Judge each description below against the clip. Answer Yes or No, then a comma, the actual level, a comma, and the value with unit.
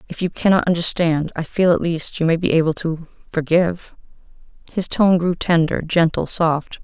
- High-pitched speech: No, medium, 170 Hz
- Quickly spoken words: No, average, 165 wpm